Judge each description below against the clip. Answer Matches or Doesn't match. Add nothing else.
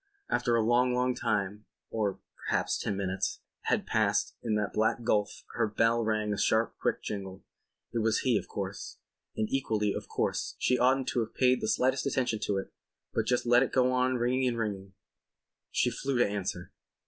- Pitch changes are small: Doesn't match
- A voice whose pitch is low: Matches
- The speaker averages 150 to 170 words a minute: Doesn't match